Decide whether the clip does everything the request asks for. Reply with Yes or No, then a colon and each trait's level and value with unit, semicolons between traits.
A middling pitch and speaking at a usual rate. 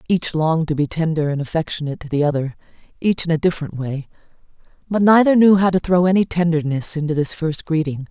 Yes: medium, 160 Hz; average, 190 wpm